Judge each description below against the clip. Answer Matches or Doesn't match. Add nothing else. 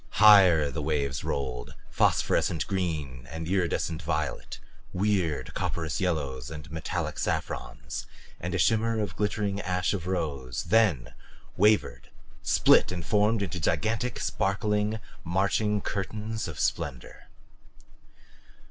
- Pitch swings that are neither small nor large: Doesn't match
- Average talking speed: Doesn't match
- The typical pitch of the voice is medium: Doesn't match